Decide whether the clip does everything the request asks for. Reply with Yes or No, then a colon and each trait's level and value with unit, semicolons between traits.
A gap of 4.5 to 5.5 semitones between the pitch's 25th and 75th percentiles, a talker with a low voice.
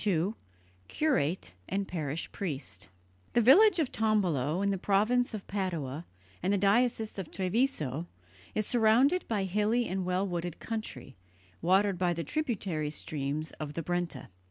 No: average, 5.2 semitones; high, 190 Hz